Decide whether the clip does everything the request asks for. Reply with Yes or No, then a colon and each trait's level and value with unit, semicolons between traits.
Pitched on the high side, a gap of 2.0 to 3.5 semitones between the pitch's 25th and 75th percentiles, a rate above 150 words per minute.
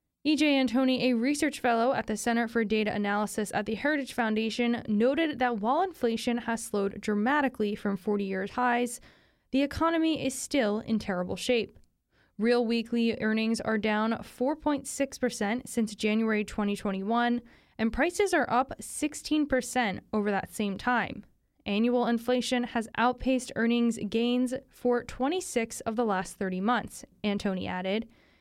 No: high, 235 Hz; average, 3.2 semitones; average, 140 wpm